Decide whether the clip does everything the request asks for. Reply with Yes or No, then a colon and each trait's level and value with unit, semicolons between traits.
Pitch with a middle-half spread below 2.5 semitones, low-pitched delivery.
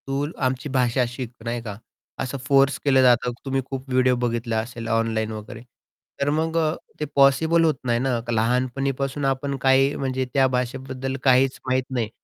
Yes: narrow, 2.0 semitones; low, 130 Hz